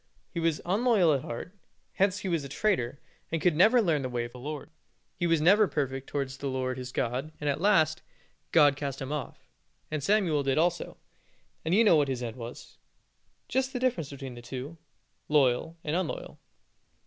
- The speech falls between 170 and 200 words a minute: Yes, average, 195 wpm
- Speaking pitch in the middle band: Yes, medium, 150 Hz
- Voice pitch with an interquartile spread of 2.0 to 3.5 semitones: No, average, 4.9 semitones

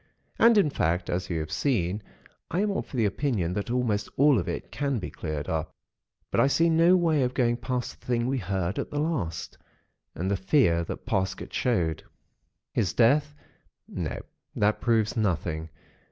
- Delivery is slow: No, average, 180 wpm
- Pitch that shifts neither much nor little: No, wide, 7.7 semitones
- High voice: No, low, 115 Hz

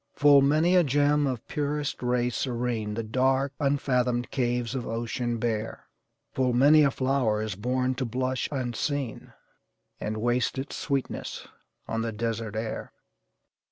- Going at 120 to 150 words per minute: Yes, average, 140 wpm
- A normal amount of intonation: Yes, average, 3.0 semitones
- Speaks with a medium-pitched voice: No, low, 125 Hz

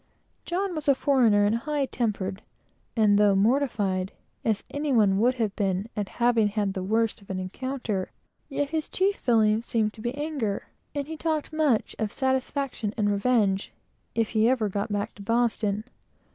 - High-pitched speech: Yes, high, 225 Hz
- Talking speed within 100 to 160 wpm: No, average, 170 wpm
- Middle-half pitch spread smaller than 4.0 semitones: No, average, 4.7 semitones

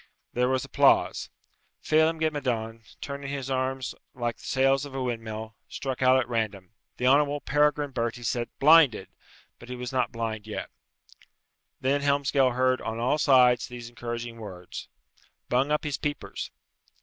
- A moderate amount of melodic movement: Yes, average, 3.1 semitones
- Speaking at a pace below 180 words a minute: Yes, average, 155 wpm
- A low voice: Yes, low, 130 Hz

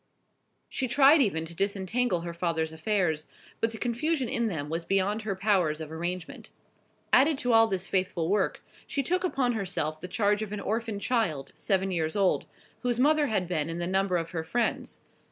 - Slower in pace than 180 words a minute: No, average, 190 wpm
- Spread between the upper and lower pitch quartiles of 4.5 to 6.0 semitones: Yes, wide, 5.5 semitones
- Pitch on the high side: Yes, high, 195 Hz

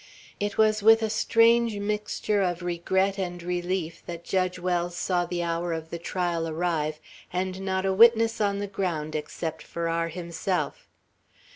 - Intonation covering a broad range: No, average, 3.0 semitones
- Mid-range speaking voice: Yes, medium, 180 Hz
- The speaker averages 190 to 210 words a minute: No, average, 155 wpm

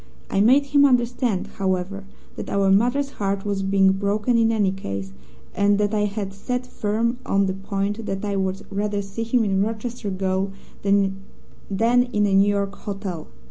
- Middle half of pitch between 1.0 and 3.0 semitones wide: Yes, average, 2.7 semitones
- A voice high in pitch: Yes, high, 200 Hz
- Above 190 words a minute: No, average, 175 wpm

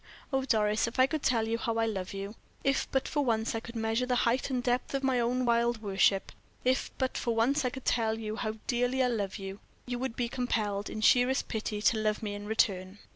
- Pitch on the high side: Yes, high, 230 Hz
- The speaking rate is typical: No, fast, 235 wpm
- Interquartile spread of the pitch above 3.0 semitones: No, average, 2.7 semitones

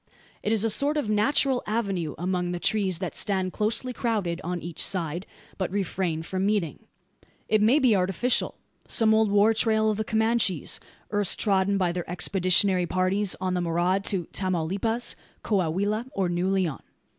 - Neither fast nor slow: Yes, average, 165 wpm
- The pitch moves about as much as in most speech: Yes, average, 3.3 semitones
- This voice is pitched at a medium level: No, high, 195 Hz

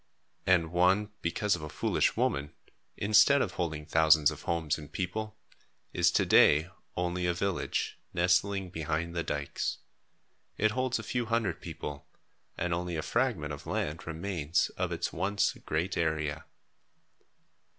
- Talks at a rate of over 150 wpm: No, average, 145 wpm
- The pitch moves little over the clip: No, average, 3.9 semitones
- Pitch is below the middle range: Yes, very low, 85 Hz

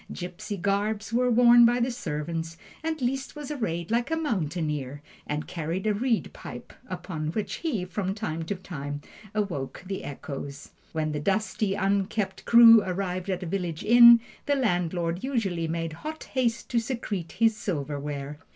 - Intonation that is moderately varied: No, wide, 6.0 semitones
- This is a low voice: No, high, 190 Hz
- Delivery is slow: No, average, 160 wpm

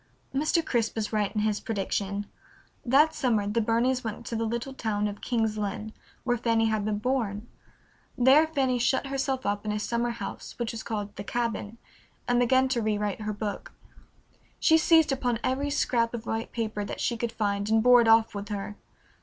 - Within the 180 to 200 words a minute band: Yes, average, 195 wpm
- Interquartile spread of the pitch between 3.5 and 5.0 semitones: No, average, 2.9 semitones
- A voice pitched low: No, high, 230 Hz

